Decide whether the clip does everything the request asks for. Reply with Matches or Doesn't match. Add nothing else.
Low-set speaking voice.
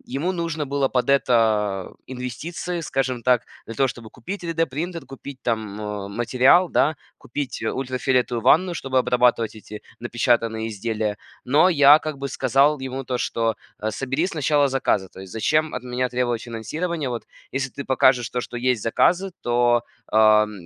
Matches